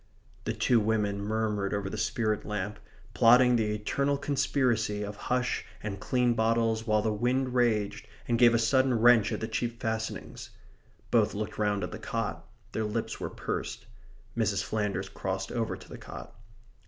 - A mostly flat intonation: Yes, narrow, 2.3 semitones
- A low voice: Yes, low, 110 Hz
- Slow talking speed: No, average, 165 wpm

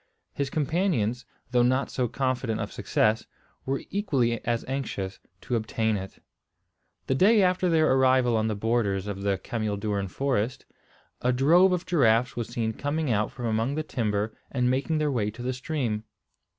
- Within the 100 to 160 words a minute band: No, average, 170 wpm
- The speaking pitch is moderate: No, low, 125 Hz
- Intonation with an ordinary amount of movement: Yes, average, 4.2 semitones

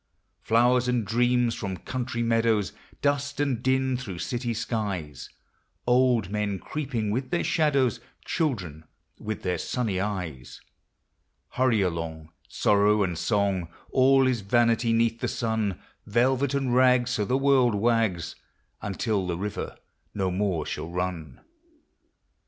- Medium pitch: No, low, 115 Hz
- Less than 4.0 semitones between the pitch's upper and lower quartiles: No, average, 4.7 semitones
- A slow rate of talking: Yes, slow, 130 wpm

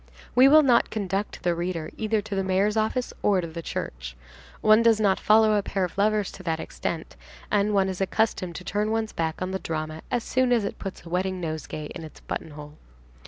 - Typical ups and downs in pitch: Yes, average, 4.3 semitones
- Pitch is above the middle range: Yes, high, 195 Hz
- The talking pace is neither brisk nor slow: No, fast, 215 wpm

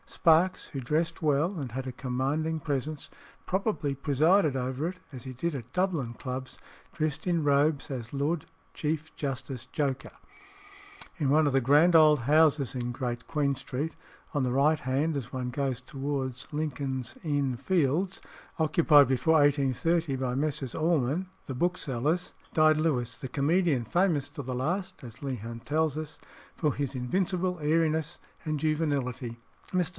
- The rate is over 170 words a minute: No, average, 155 wpm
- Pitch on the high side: No, medium, 145 Hz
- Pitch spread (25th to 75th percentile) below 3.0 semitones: No, average, 3.5 semitones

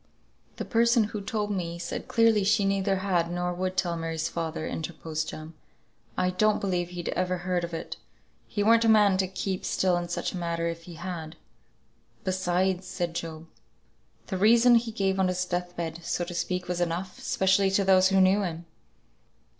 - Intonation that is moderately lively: No, narrow, 2.2 semitones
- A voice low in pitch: No, medium, 185 Hz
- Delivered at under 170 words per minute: No, average, 185 wpm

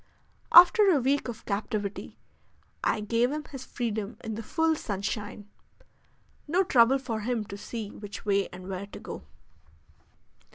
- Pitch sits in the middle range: No, high, 225 Hz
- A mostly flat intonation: No, average, 4.7 semitones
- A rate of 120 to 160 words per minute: Yes, average, 150 wpm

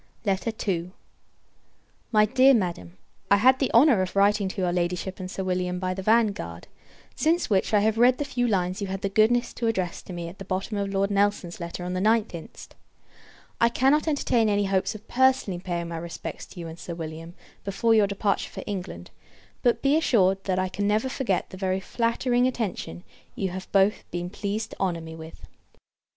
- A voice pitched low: No, high, 195 Hz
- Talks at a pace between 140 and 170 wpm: No, average, 200 wpm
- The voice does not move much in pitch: No, average, 3.8 semitones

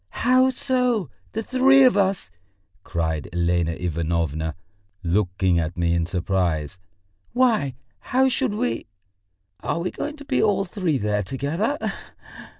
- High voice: No, low, 130 Hz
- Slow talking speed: Yes, slow, 130 wpm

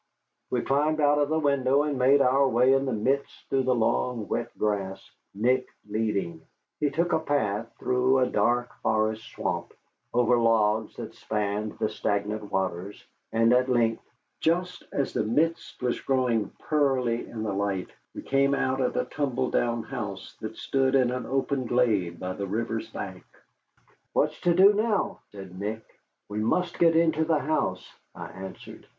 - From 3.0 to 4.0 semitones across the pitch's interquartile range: No, average, 4.5 semitones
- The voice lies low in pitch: Yes, low, 125 Hz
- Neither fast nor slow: Yes, average, 170 wpm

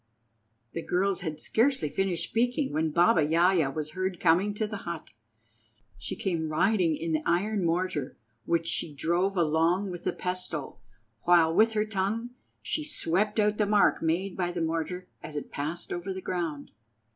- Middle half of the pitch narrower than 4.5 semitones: Yes, average, 3.5 semitones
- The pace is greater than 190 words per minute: No, average, 170 wpm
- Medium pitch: Yes, medium, 175 Hz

